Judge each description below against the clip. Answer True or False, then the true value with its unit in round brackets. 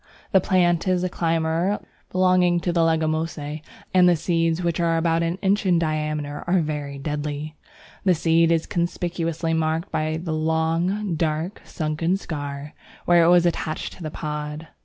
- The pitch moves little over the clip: True (2.0 semitones)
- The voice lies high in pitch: False (165 Hz)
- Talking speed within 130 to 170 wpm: True (160 wpm)